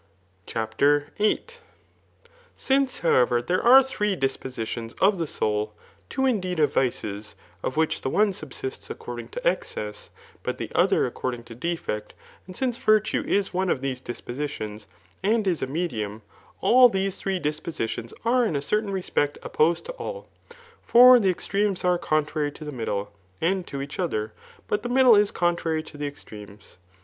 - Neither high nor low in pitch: Yes, medium, 160 Hz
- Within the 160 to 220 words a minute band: Yes, average, 165 wpm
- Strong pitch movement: Yes, wide, 8.6 semitones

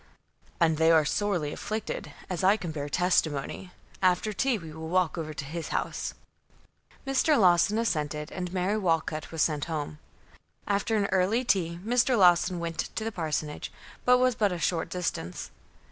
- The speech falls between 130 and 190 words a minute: Yes, average, 165 wpm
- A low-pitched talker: No, medium, 180 Hz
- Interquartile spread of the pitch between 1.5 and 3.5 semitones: No, average, 4.4 semitones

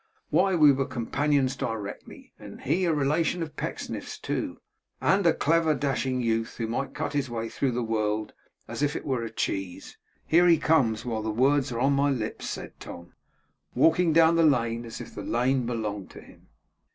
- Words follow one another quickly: No, average, 190 wpm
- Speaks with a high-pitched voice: No, low, 130 Hz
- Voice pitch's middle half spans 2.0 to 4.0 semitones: No, average, 5.1 semitones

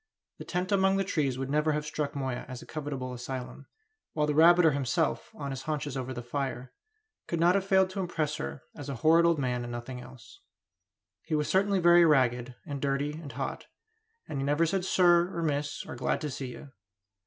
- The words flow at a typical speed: No, fast, 210 wpm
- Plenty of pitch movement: No, average, 4.4 semitones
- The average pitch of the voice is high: No, medium, 145 Hz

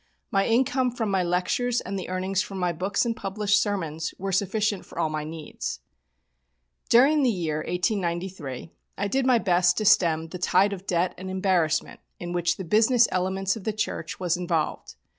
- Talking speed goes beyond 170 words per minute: Yes, average, 180 wpm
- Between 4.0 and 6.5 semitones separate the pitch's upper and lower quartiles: No, average, 3.2 semitones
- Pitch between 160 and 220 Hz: Yes, high, 190 Hz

